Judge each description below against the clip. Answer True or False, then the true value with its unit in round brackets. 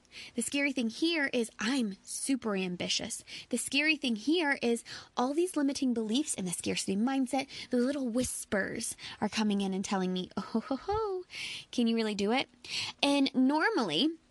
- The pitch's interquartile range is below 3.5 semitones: False (4.5 semitones)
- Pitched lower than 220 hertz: False (250 Hz)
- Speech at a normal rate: True (170 wpm)